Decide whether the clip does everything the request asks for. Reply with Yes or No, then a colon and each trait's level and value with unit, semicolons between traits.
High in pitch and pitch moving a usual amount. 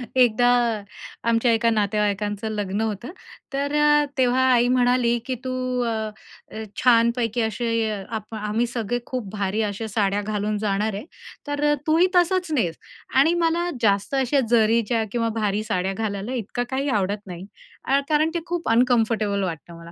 Yes: high, 230 Hz; average, 3.5 semitones